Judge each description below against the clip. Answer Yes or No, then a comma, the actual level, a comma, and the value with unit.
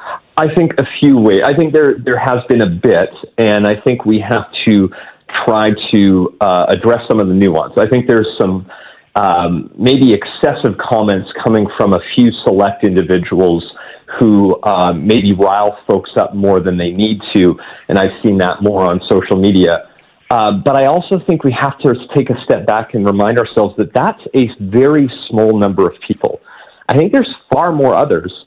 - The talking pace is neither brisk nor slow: Yes, average, 190 wpm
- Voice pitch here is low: Yes, low, 105 Hz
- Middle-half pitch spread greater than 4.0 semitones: Yes, average, 4.6 semitones